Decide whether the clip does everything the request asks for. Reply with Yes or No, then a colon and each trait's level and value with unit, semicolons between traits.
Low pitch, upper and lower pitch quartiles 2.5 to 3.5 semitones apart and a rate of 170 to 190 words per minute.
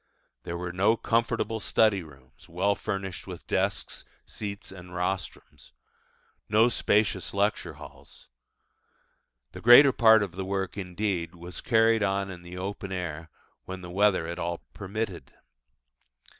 No: very low, 95 Hz; average, 3.2 semitones; slow, 135 wpm